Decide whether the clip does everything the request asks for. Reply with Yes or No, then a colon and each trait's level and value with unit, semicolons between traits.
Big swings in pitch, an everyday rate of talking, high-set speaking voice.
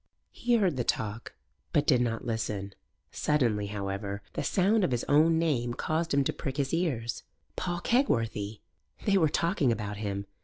No: wide, 7.6 semitones; average, 165 wpm; low, 125 Hz